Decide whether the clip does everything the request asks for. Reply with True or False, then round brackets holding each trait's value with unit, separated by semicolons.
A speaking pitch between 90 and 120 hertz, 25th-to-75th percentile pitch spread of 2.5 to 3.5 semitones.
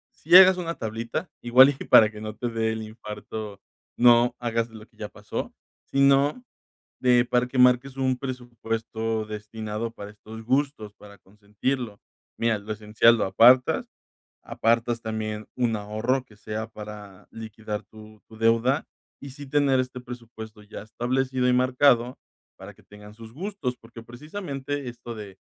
True (115 Hz; 2.9 semitones)